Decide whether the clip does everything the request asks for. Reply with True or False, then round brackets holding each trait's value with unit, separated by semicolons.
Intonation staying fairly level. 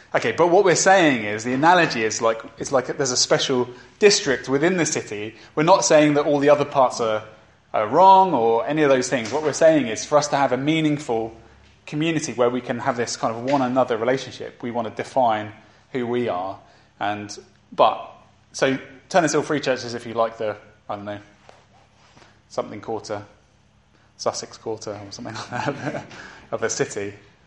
False (4.7 semitones)